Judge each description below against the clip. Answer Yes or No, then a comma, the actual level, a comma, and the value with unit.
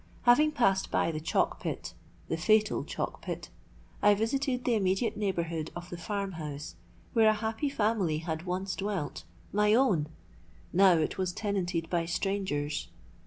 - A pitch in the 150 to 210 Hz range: Yes, high, 190 Hz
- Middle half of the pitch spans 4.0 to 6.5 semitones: Yes, average, 4.5 semitones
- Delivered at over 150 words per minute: No, average, 140 wpm